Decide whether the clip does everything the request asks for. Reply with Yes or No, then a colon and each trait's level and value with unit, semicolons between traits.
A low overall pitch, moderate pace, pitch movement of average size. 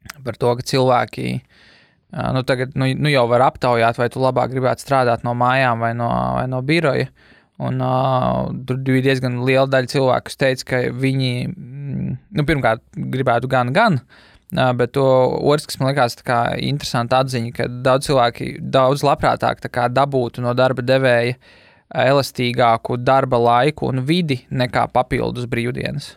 No: low, 130 Hz; average, 150 wpm; narrow, 1.7 semitones